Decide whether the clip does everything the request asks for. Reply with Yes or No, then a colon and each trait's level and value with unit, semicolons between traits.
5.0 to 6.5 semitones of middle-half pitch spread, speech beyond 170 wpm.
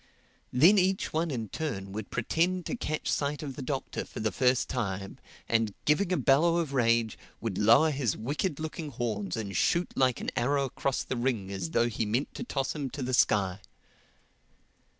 Yes: wide, 5.4 semitones; average, 190 wpm